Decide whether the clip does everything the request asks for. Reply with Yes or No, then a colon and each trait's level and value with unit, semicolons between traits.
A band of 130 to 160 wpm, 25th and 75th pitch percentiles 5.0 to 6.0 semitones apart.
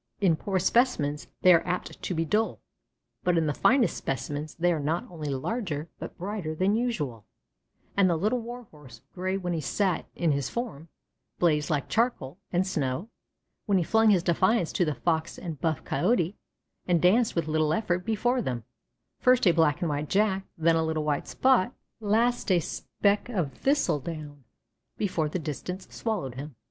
No: average, 180 wpm; wide, 5.4 semitones